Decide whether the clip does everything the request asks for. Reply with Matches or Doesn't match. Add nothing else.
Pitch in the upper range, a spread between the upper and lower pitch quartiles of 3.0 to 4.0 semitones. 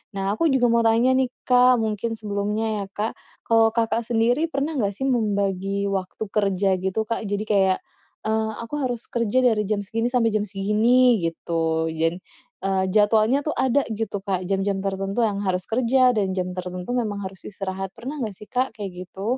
Matches